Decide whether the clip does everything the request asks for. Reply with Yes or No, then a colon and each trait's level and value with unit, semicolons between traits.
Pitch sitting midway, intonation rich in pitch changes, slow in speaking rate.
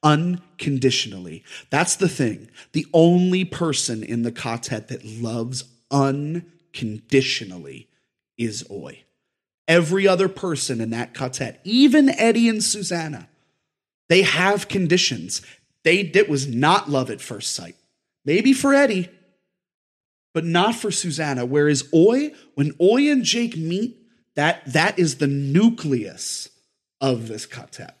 Yes: medium, 160 Hz; wide, 6.6 semitones; slow, 125 wpm